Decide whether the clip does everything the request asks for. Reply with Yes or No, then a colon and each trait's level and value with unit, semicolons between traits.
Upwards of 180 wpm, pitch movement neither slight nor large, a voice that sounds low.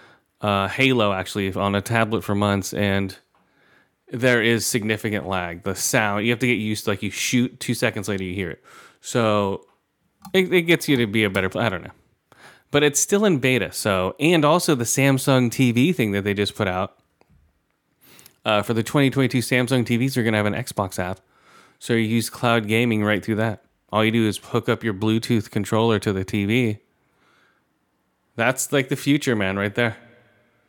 Yes: average, 195 wpm; average, 3.5 semitones; low, 115 Hz